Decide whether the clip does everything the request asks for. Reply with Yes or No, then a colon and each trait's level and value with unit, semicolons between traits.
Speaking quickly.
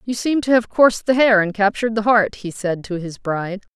Yes: fast, 255 wpm